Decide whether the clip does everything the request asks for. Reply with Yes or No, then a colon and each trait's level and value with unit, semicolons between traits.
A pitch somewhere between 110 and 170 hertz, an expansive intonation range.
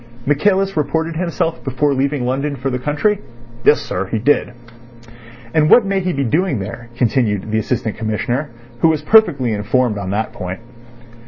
Yes: low, 135 Hz; wide, 6.0 semitones